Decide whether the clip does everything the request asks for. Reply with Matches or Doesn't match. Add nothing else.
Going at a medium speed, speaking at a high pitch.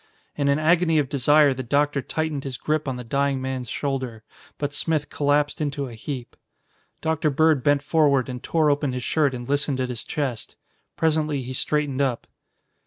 Doesn't match